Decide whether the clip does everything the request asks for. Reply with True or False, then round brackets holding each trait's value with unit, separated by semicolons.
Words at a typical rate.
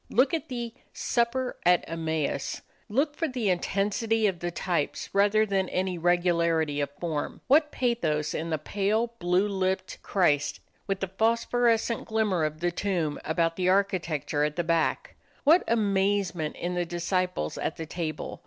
True (160 wpm)